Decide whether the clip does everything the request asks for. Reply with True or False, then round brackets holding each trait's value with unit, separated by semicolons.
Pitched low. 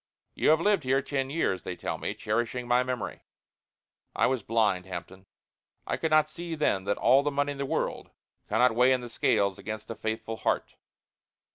True (125 Hz)